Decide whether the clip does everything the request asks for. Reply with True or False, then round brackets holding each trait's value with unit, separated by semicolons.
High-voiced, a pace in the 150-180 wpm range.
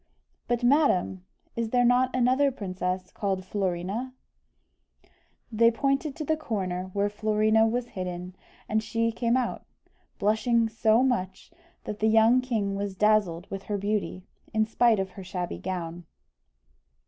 False (215 Hz; 140 wpm)